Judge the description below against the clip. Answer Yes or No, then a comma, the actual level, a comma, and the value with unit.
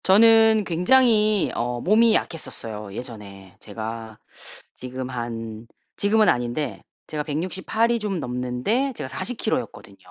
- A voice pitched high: No, medium, 150 Hz